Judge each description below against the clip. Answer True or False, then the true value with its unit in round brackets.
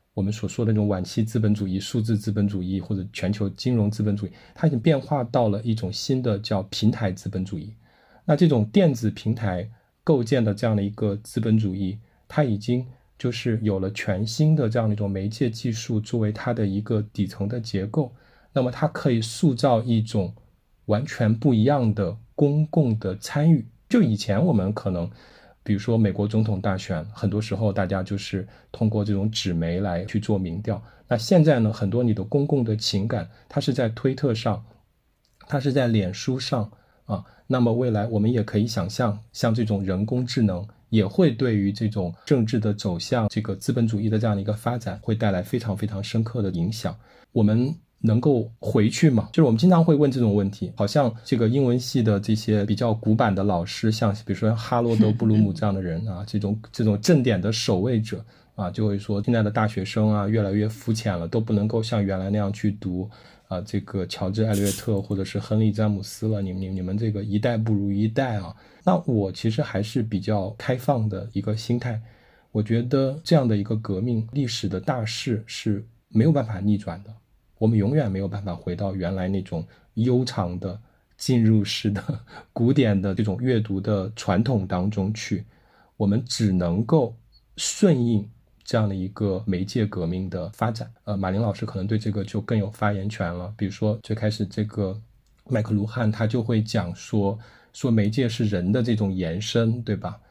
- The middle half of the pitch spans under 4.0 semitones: True (2.9 semitones)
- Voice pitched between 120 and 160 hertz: False (110 Hz)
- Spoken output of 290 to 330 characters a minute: True (295 characters per minute)